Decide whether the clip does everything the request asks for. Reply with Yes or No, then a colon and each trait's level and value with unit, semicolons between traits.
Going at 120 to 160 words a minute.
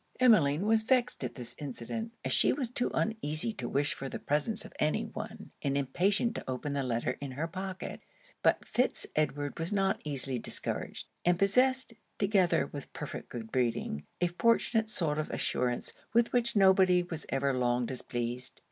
No: average, 175 wpm